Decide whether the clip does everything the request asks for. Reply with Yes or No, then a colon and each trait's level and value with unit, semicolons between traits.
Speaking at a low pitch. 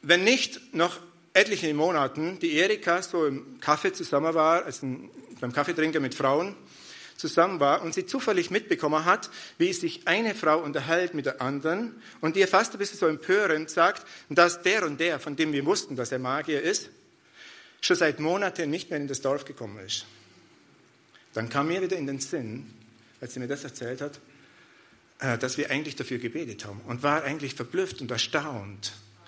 No: medium, 155 Hz